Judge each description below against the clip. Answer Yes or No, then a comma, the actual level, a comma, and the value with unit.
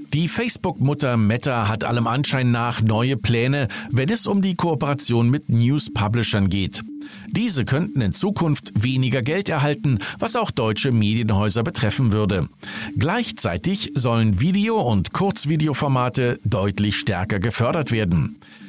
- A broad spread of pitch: Yes, wide, 6.0 semitones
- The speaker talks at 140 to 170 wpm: No, slow, 125 wpm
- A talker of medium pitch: No, low, 125 Hz